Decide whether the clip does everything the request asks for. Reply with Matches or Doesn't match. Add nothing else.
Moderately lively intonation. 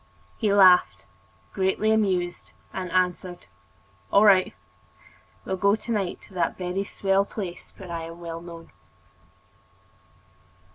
Doesn't match